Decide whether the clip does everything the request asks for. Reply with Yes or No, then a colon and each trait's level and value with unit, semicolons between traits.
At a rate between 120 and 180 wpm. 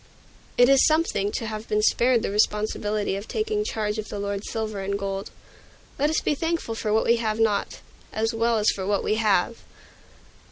No: average, 195 wpm